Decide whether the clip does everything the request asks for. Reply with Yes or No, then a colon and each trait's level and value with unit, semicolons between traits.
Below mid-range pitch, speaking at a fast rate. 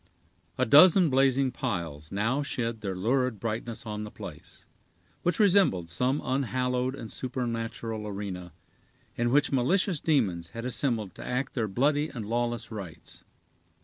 No: low, 120 Hz; average, 140 wpm